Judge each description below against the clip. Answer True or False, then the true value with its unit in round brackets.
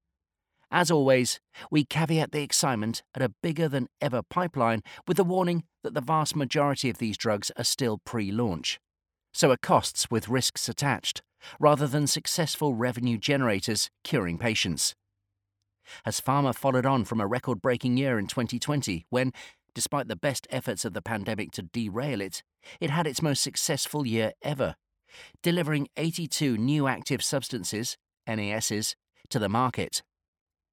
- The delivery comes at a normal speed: True (150 wpm)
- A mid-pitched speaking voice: False (125 Hz)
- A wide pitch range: False (5.0 semitones)